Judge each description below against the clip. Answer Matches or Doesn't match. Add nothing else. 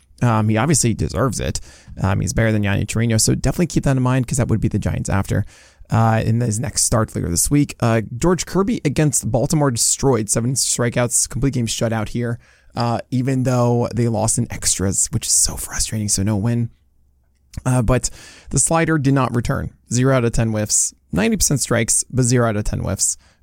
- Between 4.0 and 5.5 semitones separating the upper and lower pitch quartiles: Doesn't match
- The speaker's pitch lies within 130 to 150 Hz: Doesn't match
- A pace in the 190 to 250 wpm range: Matches